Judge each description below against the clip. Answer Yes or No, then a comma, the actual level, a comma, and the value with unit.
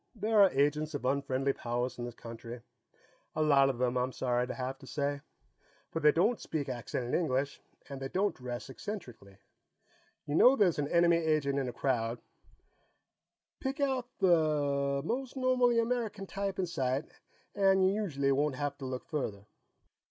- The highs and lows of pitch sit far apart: Yes, wide, 6.7 semitones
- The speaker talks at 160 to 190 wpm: Yes, average, 165 wpm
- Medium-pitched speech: Yes, medium, 145 Hz